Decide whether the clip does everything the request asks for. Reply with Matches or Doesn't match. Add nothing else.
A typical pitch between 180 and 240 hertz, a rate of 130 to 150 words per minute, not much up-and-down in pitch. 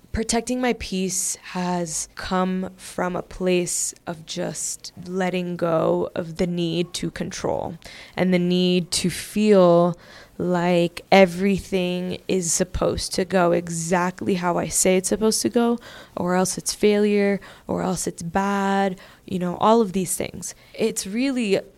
Matches